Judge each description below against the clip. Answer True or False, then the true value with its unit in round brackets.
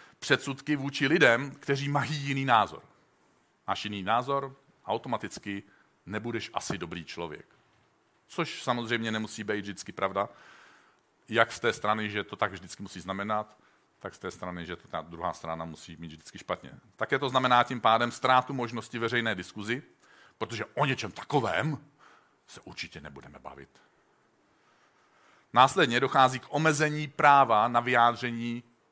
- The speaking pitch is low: True (115 Hz)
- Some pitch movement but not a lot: True (4.9 semitones)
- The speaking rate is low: False (140 wpm)